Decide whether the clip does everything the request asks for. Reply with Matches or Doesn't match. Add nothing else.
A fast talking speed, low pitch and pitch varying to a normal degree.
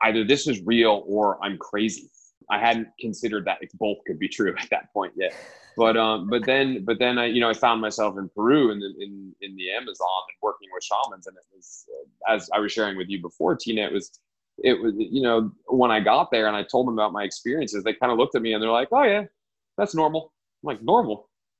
Matches